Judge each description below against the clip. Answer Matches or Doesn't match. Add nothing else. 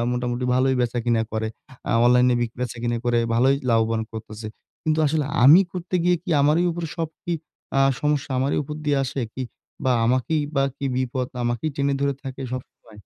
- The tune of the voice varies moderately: Matches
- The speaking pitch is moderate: Doesn't match